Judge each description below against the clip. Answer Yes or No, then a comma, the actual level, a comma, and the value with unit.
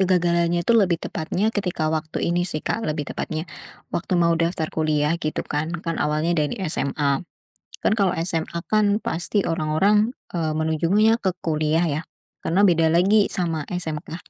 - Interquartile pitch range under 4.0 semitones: Yes, average, 2.9 semitones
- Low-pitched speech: No, medium, 170 Hz